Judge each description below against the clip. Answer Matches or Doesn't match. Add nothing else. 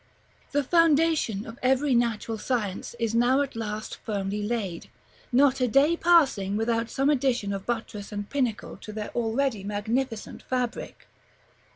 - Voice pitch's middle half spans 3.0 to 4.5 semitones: Matches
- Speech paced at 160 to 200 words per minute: Doesn't match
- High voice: Matches